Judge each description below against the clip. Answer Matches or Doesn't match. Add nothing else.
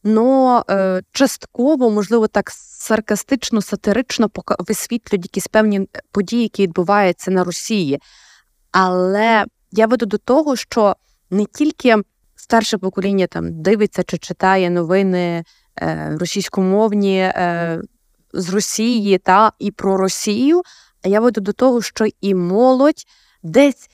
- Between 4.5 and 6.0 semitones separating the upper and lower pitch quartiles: Doesn't match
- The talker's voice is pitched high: Matches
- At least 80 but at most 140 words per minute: Matches